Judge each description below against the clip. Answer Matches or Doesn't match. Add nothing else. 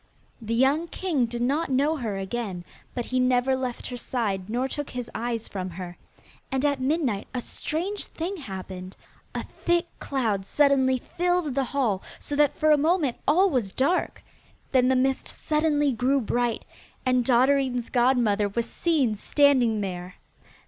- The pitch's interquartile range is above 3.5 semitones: Matches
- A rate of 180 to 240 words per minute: Doesn't match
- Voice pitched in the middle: Doesn't match